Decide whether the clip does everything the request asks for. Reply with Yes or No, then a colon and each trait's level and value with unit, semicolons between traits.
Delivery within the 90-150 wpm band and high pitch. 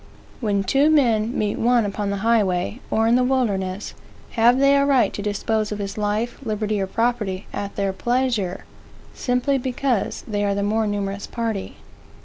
No: average, 170 wpm; high, 215 Hz